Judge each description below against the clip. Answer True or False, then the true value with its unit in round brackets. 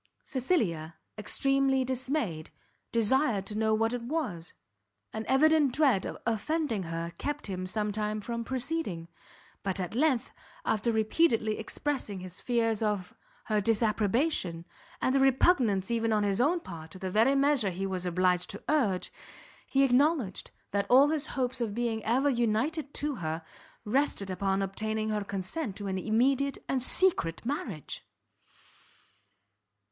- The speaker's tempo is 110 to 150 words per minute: True (145 wpm)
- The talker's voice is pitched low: False (225 Hz)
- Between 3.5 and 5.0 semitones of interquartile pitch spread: False (5.6 semitones)